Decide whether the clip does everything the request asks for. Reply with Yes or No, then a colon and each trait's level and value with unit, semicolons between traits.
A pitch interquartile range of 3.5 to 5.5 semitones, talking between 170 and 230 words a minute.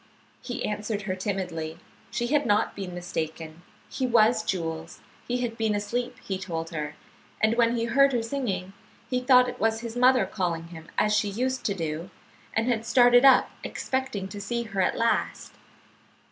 Yes: average, 4.9 semitones; average, 175 wpm